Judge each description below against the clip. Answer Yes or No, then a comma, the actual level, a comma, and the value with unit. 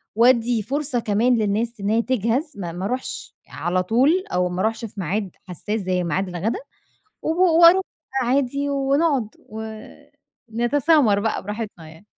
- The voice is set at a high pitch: Yes, high, 225 Hz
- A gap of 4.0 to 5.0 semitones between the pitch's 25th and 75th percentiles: Yes, average, 4.6 semitones